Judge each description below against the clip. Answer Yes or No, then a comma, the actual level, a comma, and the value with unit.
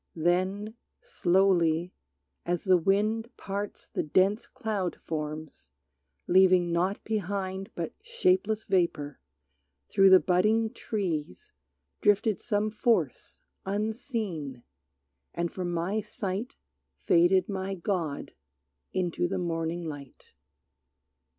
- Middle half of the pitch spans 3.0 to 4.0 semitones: Yes, average, 3.5 semitones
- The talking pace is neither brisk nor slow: No, slow, 100 wpm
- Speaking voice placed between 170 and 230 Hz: Yes, high, 190 Hz